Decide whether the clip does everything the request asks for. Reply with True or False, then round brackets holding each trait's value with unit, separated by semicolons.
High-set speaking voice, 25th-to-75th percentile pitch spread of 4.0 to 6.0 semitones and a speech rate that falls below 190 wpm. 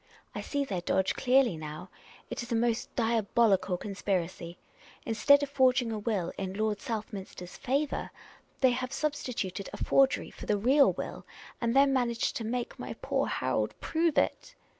True (230 Hz; 5.0 semitones; 165 wpm)